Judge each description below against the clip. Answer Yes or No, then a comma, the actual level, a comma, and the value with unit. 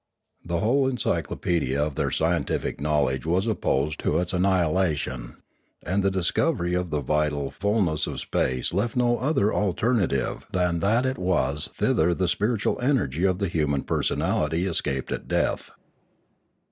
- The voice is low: Yes, very low, 90 Hz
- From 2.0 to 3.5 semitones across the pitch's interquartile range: No, average, 5.2 semitones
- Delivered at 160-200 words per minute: No, average, 145 wpm